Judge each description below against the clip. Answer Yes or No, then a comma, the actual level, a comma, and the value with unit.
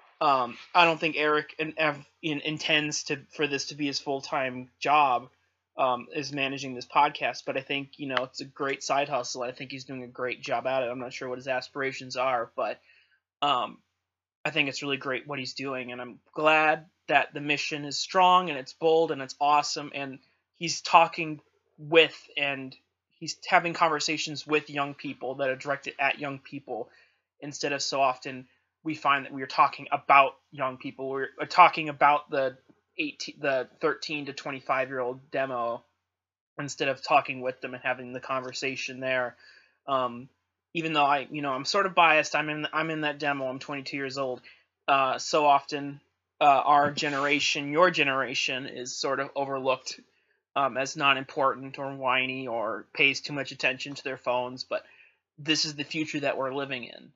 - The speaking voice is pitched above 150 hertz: No, medium, 140 Hz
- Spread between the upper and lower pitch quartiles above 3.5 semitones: No, narrow, 2.5 semitones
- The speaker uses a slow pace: No, average, 185 wpm